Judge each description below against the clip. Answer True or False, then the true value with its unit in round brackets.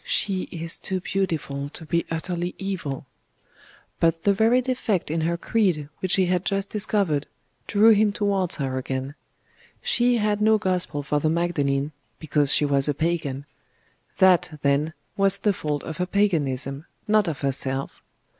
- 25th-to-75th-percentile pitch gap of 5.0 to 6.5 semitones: True (5.4 semitones)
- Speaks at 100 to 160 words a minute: True (155 wpm)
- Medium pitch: True (170 Hz)